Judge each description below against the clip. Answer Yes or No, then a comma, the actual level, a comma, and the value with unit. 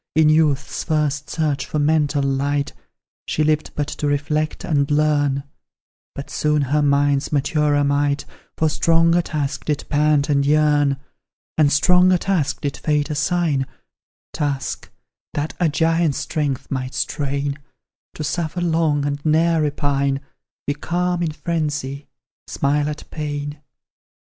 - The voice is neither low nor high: Yes, medium, 150 Hz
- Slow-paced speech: Yes, slow, 130 wpm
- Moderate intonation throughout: No, narrow, 1.5 semitones